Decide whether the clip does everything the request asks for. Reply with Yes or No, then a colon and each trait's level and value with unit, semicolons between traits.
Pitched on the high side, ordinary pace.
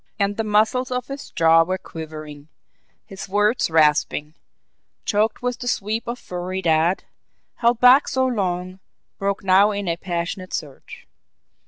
Yes: high, 195 Hz; average, 145 wpm